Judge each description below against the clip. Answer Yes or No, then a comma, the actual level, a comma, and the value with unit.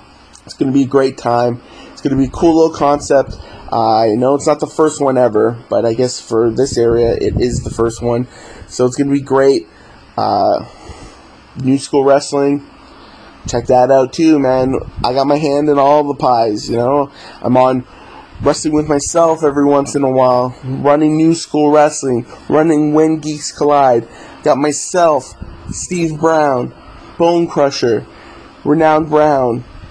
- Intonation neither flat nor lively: Yes, average, 3.6 semitones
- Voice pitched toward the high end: No, medium, 140 Hz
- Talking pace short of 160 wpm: No, average, 175 wpm